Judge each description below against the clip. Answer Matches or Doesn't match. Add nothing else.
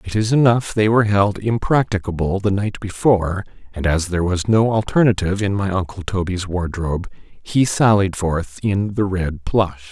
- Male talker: Matches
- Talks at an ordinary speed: Matches